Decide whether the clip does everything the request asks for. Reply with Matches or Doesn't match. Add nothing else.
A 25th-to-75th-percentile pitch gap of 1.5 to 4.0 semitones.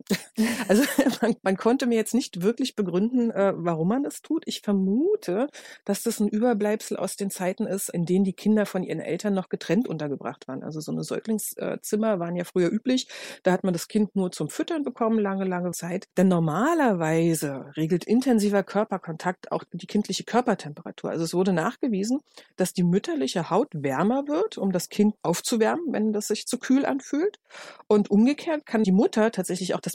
Doesn't match